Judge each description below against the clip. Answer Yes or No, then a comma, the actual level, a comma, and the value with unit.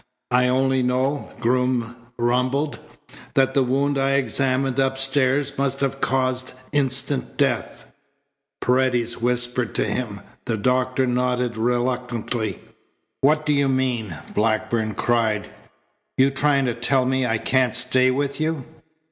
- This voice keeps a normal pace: No, slow, 125 wpm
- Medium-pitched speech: No, low, 130 Hz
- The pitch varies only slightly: Yes, narrow, 1.7 semitones